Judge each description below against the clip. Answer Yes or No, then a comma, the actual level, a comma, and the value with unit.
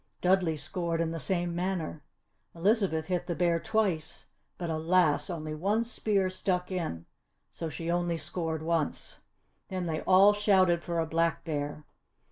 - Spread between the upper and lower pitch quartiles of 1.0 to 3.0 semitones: Yes, narrow, 2.5 semitones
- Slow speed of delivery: No, average, 150 wpm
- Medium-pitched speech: Yes, medium, 170 Hz